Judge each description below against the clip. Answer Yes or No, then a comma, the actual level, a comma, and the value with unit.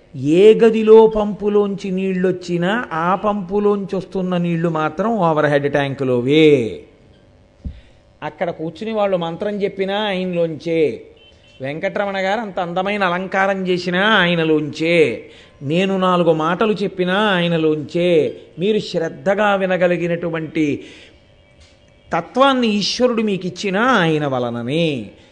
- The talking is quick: No, average, 90 wpm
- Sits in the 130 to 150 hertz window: No, medium, 185 Hz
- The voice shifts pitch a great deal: No, average, 3.8 semitones